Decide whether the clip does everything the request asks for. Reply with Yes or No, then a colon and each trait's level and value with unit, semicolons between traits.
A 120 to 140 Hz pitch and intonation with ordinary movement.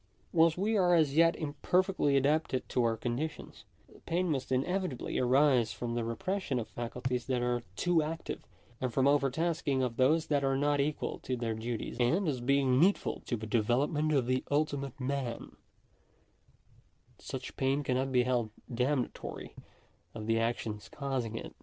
Yes: low, 135 Hz; average, 3.9 semitones